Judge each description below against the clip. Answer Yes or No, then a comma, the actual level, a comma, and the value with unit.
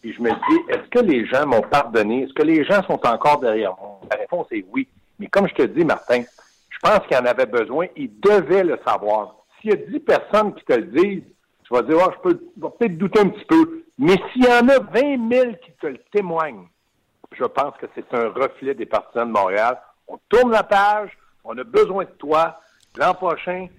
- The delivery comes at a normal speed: No, fast, 235 wpm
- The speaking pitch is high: Yes, high, 210 Hz